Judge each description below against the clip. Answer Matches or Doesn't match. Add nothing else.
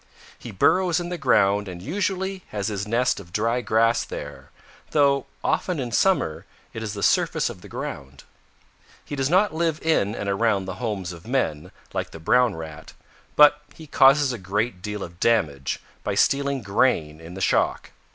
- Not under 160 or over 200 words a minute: Matches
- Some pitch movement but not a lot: Doesn't match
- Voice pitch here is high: Doesn't match